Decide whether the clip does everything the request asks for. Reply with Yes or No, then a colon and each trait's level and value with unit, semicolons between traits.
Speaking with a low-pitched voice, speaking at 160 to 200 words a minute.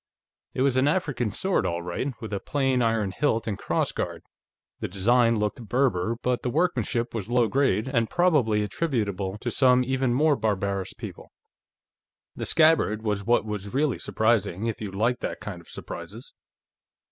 Yes: low, 115 Hz; average, 170 wpm